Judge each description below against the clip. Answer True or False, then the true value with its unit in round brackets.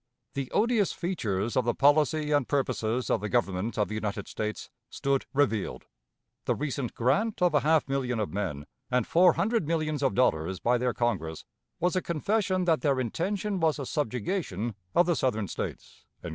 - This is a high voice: False (135 Hz)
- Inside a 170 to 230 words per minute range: True (175 wpm)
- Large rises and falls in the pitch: True (6.7 semitones)